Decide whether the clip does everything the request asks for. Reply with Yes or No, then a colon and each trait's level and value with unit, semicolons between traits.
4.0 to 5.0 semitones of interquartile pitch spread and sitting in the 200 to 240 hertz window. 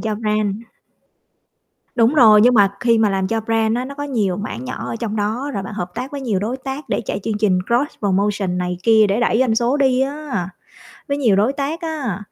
Yes: average, 4.3 semitones; high, 225 Hz